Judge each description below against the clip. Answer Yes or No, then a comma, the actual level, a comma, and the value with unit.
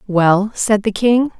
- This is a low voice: No, high, 210 Hz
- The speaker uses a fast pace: No, average, 170 wpm